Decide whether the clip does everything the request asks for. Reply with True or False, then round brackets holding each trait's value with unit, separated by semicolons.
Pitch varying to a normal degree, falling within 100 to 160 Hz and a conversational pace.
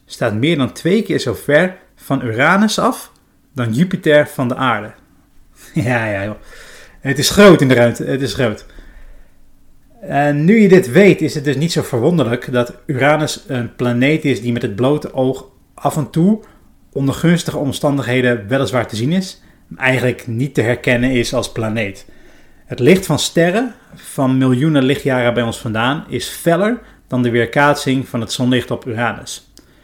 True (4.2 semitones; 135 Hz; 175 wpm)